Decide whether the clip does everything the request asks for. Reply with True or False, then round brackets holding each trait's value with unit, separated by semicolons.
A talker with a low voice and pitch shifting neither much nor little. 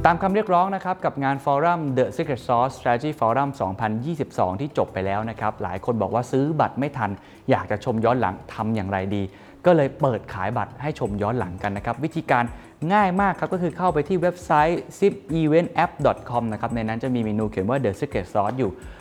False (130 Hz; 6.7 semitones)